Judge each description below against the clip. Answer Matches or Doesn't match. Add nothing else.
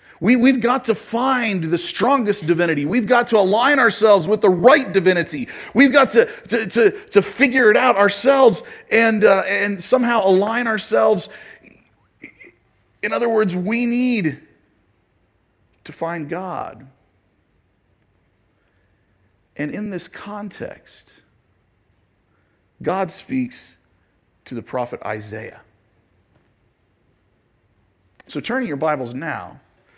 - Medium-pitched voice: Matches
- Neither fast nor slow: Doesn't match